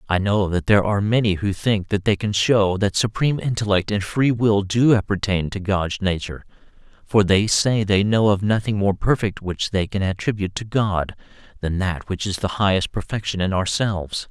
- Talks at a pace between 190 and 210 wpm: Yes, average, 195 wpm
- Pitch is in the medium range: No, low, 100 Hz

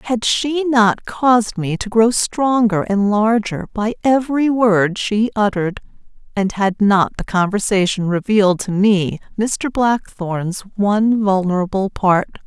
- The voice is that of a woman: Yes, female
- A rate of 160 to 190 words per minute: No, slow, 135 wpm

